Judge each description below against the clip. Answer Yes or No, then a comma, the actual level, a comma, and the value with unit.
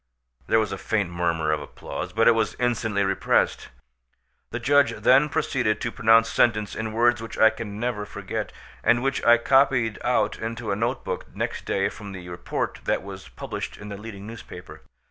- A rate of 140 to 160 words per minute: No, average, 185 wpm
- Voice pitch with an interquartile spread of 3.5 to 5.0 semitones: No, average, 2.8 semitones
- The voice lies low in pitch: Yes, low, 110 Hz